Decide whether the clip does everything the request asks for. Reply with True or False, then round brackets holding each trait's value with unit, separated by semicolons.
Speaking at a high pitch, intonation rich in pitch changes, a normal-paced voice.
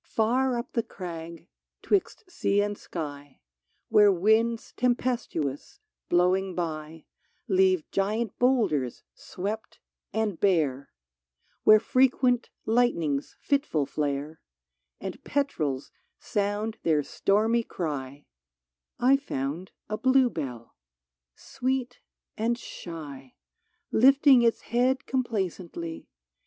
False (200 Hz; 7.4 semitones; 95 wpm)